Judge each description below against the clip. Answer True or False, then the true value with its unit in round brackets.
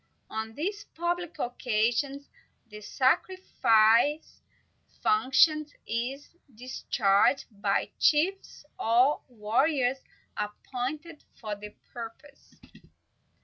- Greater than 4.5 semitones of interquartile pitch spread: True (5.3 semitones)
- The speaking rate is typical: False (80 wpm)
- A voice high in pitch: True (255 Hz)